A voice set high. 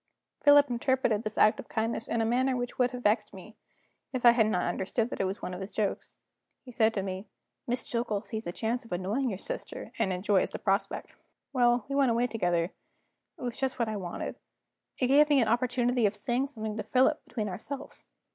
Yes: high, 230 Hz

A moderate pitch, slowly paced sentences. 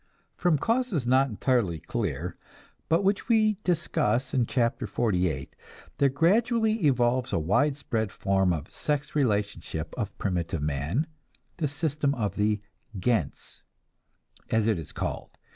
No: low, 120 Hz; slow, 125 wpm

